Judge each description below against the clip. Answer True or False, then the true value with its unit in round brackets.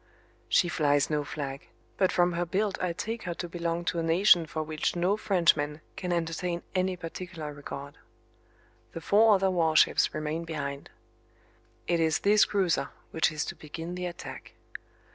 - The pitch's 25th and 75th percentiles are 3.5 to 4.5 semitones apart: False (2.7 semitones)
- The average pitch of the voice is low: False (170 Hz)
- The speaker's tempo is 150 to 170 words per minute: True (160 wpm)